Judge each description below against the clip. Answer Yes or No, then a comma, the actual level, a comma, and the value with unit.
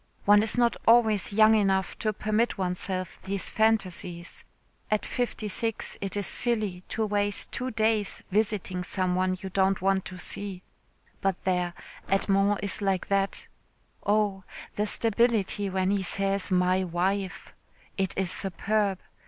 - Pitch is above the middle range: Yes, high, 195 Hz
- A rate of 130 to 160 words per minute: Yes, average, 145 wpm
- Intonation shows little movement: Yes, narrow, 2.3 semitones